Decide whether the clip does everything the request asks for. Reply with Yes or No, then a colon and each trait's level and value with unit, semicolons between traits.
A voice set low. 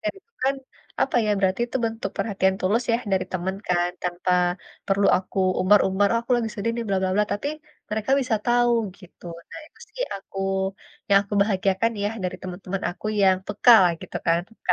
No: high, 200 Hz